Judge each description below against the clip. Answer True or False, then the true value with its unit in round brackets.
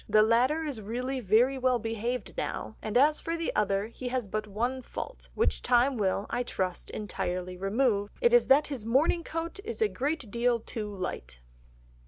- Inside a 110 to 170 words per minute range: False (185 wpm)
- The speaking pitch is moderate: False (240 Hz)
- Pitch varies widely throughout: False (4.5 semitones)